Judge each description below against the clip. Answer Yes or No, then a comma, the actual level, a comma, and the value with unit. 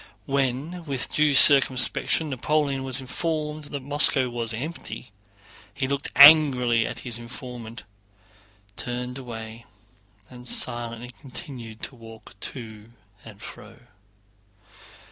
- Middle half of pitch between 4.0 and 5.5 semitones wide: No, average, 3.2 semitones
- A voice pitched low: Yes, low, 125 Hz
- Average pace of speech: No, slow, 105 wpm